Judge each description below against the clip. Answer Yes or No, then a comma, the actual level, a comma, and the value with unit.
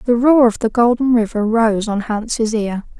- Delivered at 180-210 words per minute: Yes, average, 200 wpm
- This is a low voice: No, high, 225 Hz